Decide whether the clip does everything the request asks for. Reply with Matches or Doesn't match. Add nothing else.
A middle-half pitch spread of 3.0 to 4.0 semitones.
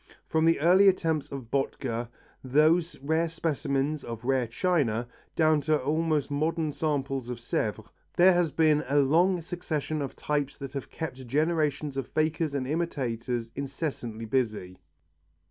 Matches